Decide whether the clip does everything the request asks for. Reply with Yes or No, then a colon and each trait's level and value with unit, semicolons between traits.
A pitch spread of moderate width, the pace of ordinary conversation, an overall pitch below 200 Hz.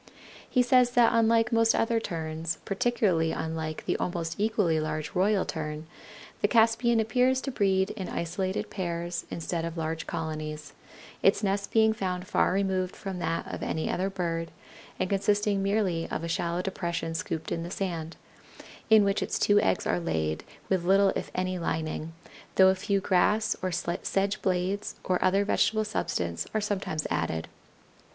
Yes: average, 3.8 semitones; average, 160 wpm; medium, 185 Hz